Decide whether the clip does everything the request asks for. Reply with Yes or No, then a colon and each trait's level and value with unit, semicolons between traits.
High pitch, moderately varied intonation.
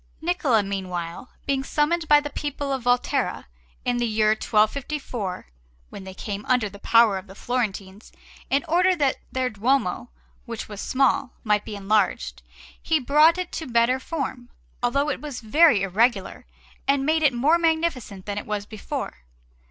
No: high, 245 Hz; wide, 5.8 semitones